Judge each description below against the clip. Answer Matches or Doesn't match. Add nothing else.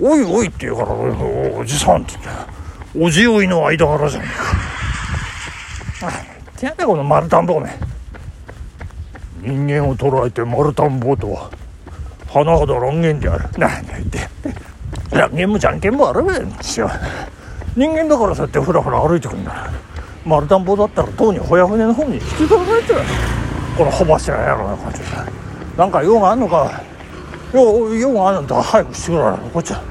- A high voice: Doesn't match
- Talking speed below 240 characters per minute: Doesn't match